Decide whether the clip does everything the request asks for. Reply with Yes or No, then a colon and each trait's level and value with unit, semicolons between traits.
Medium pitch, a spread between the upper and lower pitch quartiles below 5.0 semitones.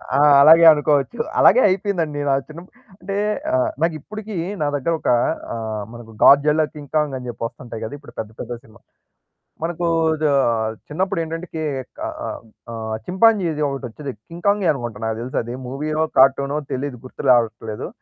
Yes: medium, 150 Hz; average, 4.6 semitones